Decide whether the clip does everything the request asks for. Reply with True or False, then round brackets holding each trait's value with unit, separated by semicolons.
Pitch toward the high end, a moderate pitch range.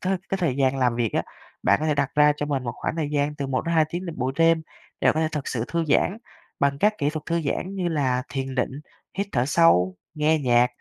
False (145 Hz; 3.9 semitones)